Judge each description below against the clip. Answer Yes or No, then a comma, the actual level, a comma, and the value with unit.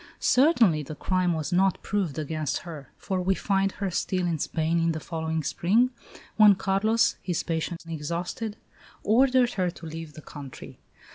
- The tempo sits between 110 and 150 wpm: No, average, 160 wpm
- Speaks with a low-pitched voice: No, medium, 175 Hz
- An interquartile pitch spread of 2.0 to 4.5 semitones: Yes, average, 3.7 semitones